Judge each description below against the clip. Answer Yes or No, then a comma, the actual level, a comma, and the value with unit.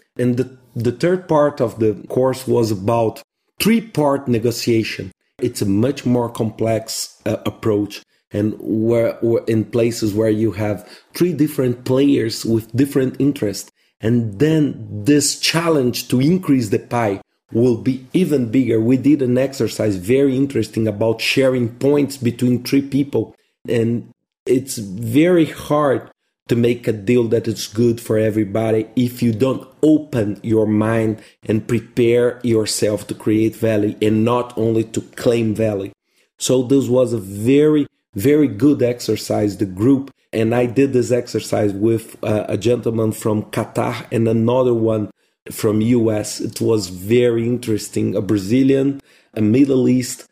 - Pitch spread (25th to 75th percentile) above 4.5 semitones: No, average, 3.0 semitones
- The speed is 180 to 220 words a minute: No, average, 145 wpm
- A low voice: Yes, low, 120 Hz